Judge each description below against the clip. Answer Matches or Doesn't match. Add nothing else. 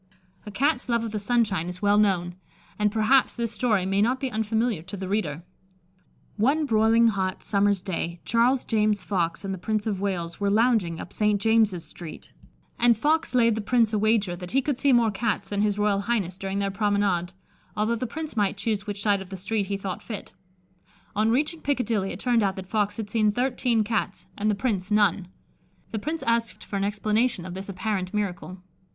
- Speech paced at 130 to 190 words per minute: Doesn't match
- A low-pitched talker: Doesn't match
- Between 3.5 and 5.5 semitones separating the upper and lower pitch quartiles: Doesn't match